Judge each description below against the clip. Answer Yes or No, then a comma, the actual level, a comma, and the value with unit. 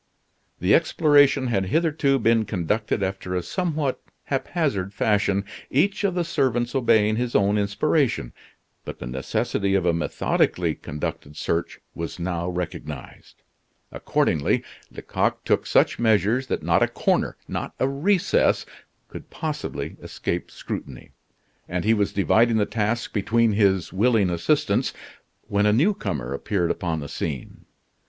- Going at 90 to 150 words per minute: Yes, slow, 135 wpm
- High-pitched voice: No, low, 105 Hz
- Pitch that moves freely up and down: Yes, wide, 6.6 semitones